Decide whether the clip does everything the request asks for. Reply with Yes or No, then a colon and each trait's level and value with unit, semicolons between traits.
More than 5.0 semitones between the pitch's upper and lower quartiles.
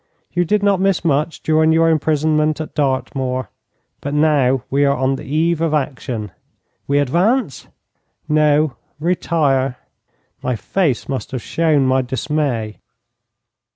No: average, 3.3 semitones